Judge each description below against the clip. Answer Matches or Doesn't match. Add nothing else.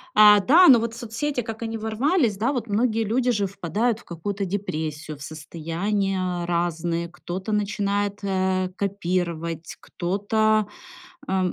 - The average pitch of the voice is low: Doesn't match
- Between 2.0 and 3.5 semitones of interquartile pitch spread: Doesn't match